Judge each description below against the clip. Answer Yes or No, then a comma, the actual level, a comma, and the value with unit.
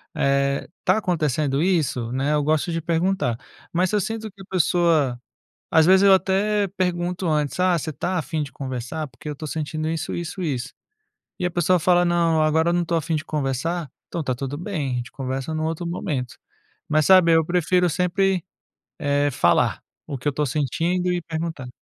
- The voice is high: No, medium, 160 Hz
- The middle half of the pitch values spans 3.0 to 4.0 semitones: Yes, average, 3.7 semitones